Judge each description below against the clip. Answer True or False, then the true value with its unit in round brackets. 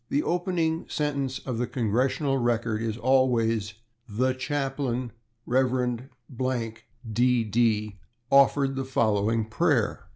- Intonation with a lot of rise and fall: False (3.0 semitones)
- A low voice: True (125 Hz)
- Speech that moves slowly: True (100 wpm)